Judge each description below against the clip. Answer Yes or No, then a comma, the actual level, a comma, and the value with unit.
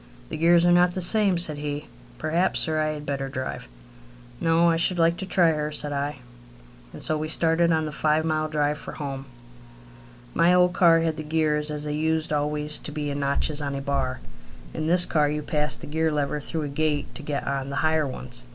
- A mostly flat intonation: Yes, narrow, 2.0 semitones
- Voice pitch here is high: No, medium, 155 Hz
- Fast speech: Yes, fast, 220 wpm